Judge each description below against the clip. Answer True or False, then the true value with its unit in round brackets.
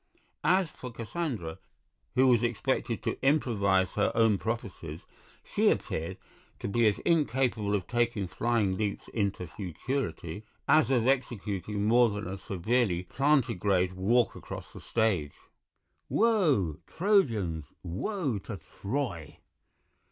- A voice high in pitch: False (110 Hz)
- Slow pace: True (120 wpm)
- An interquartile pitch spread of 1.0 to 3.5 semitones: False (5.1 semitones)